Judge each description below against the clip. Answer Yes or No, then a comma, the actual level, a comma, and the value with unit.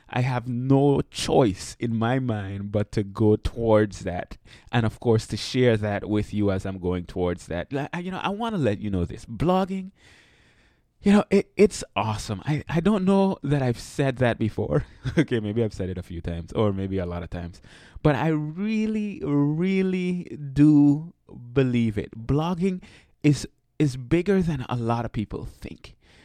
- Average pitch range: No, wide, 6.5 semitones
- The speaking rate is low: No, average, 185 wpm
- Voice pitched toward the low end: Yes, low, 120 Hz